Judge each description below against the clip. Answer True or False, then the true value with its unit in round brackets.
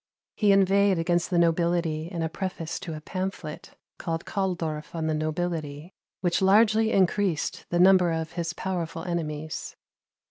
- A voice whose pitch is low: False (170 Hz)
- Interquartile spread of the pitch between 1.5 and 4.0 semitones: True (2.8 semitones)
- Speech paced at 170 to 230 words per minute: False (145 wpm)